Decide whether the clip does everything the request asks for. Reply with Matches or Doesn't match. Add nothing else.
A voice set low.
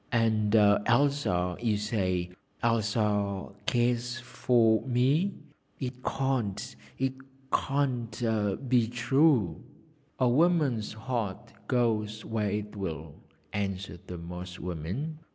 Matches